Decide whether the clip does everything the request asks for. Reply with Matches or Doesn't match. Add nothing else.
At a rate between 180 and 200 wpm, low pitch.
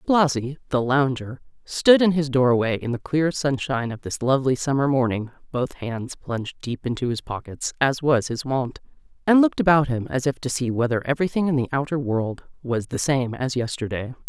Matches